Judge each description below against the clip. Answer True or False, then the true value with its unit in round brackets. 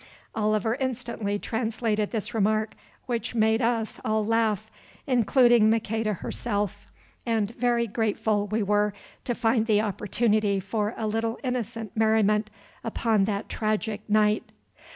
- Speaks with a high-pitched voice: True (220 Hz)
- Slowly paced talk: True (125 wpm)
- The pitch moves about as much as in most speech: False (1.5 semitones)